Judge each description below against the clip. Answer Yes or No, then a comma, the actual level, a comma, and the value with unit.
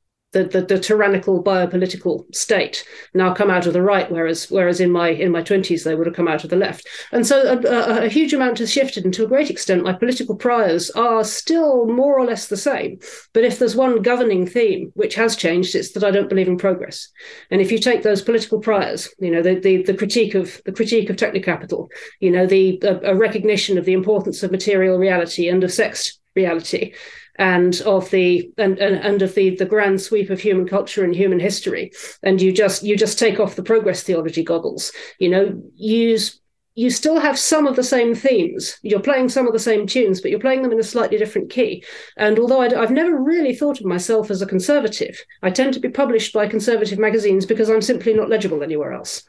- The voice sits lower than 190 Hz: No, high, 210 Hz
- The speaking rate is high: Yes, fast, 225 wpm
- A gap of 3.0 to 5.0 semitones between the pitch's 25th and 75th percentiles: Yes, average, 4.2 semitones